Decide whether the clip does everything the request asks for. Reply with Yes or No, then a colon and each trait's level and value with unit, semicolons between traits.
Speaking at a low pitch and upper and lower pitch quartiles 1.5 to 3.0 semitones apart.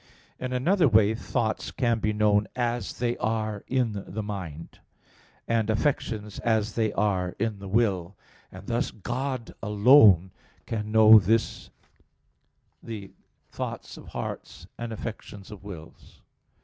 Yes: low, 110 Hz; narrow, 2.5 semitones